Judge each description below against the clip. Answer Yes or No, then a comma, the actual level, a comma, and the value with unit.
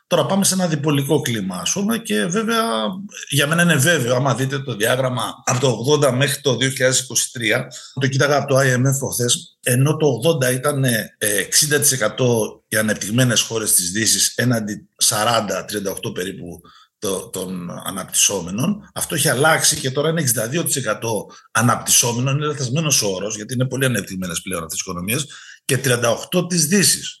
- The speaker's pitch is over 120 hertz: Yes, low, 135 Hz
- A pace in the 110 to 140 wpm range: No, average, 150 wpm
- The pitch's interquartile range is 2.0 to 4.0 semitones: No, average, 4.8 semitones